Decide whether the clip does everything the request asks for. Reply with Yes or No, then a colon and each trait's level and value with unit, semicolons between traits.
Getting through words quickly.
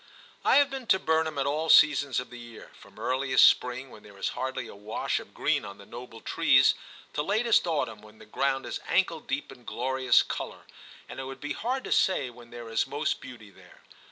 Yes: fast, 215 wpm